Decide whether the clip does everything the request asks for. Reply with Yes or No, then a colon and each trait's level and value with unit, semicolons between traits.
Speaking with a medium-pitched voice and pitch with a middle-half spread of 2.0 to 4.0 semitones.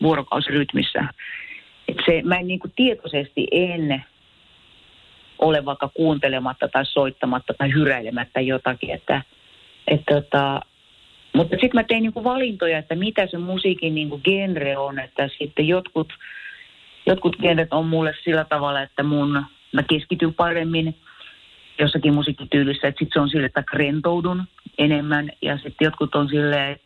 Yes: medium, 155 Hz; average, 3.4 semitones